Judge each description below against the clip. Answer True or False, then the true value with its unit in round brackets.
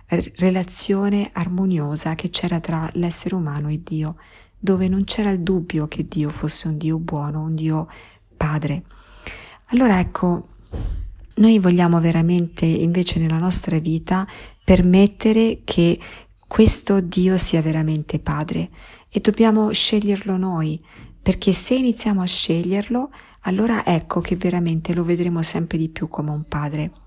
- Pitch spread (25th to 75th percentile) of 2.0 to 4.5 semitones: True (3.1 semitones)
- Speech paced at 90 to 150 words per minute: True (135 wpm)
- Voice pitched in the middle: True (175 Hz)